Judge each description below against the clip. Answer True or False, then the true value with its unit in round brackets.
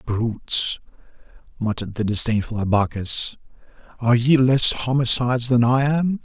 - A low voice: True (120 Hz)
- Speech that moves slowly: True (115 wpm)